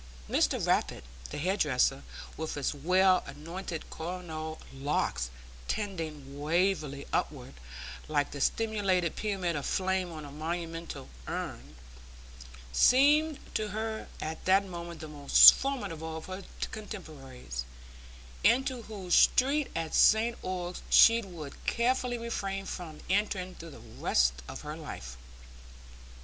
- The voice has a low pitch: No, medium, 175 Hz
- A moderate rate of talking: No, slow, 125 wpm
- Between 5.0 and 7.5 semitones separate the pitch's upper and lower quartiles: Yes, average, 5.3 semitones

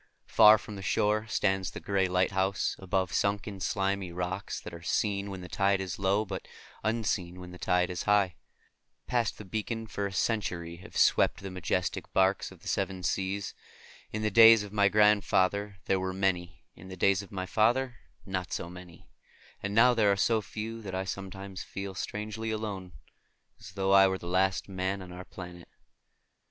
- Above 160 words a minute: Yes, average, 185 wpm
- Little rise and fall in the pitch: Yes, narrow, 2.1 semitones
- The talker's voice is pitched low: Yes, very low, 95 Hz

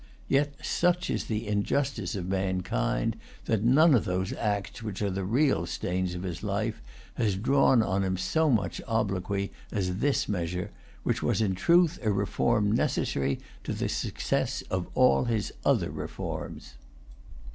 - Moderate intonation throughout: Yes, average, 4.2 semitones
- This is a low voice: Yes, low, 105 Hz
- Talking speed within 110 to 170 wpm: Yes, average, 155 wpm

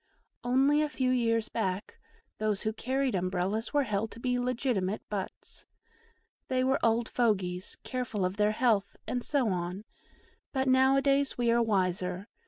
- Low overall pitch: No, high, 230 Hz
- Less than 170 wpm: Yes, average, 160 wpm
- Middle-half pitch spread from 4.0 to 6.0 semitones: Yes, average, 4.6 semitones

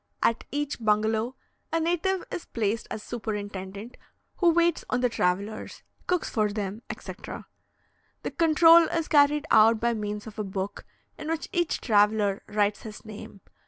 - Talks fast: No, average, 155 wpm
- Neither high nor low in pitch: No, high, 220 Hz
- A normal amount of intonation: No, wide, 6.8 semitones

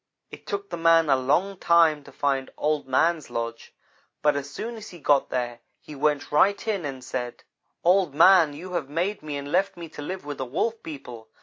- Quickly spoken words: Yes, fast, 210 wpm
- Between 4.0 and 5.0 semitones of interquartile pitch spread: Yes, average, 4.4 semitones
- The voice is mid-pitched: Yes, medium, 150 Hz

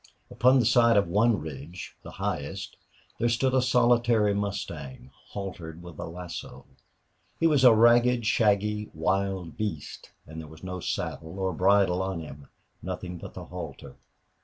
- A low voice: Yes, very low, 95 Hz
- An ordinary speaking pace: Yes, average, 155 wpm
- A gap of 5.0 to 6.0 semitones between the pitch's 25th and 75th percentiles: Yes, wide, 5.6 semitones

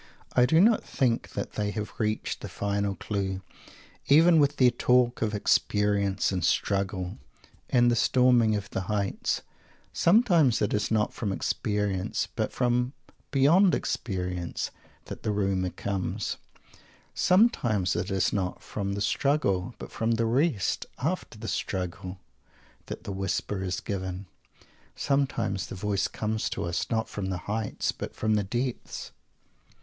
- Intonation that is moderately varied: Yes, average, 4.2 semitones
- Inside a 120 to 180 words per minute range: Yes, average, 145 wpm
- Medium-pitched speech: No, low, 105 Hz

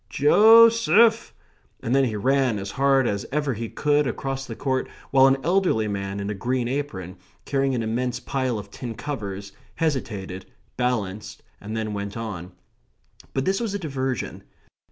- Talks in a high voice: No, low, 125 Hz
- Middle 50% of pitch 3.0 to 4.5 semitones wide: No, average, 5.0 semitones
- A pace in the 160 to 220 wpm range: Yes, average, 165 wpm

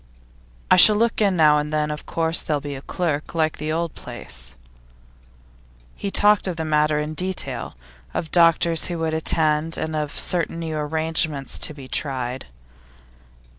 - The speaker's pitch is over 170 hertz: No, medium, 155 Hz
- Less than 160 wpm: No, average, 170 wpm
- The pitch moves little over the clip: Yes, narrow, 1.8 semitones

